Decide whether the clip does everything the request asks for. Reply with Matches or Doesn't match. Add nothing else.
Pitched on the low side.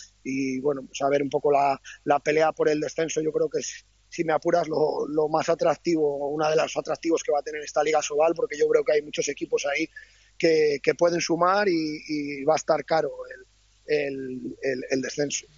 Doesn't match